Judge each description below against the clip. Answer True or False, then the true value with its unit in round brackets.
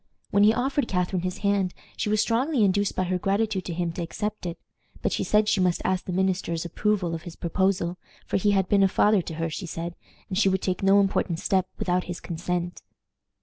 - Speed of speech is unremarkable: False (225 wpm)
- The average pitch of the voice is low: False (185 Hz)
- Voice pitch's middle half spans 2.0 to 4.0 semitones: True (2.5 semitones)